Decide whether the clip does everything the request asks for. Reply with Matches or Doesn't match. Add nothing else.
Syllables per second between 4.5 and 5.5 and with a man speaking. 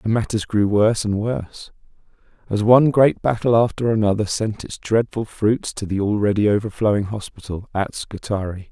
Matches